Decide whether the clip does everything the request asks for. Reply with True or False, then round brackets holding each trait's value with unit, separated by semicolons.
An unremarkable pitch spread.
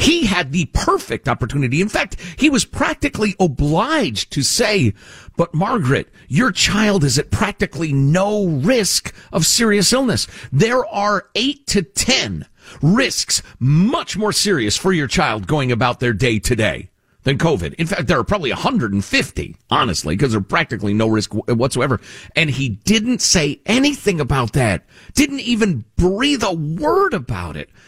False (8.8 semitones)